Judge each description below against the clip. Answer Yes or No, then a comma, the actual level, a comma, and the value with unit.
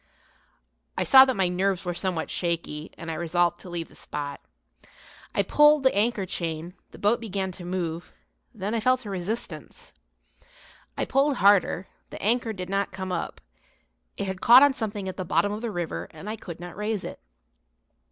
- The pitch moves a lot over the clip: No, average, 4.1 semitones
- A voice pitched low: No, high, 190 Hz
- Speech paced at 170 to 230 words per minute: Yes, average, 185 wpm